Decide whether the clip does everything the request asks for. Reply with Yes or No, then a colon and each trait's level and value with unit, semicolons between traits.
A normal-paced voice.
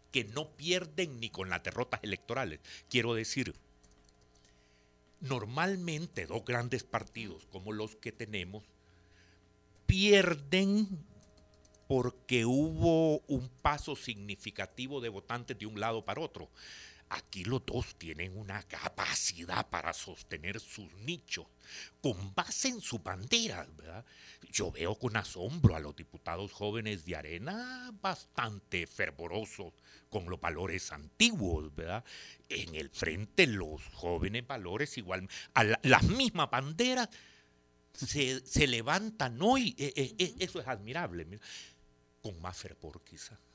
No: slow, 120 wpm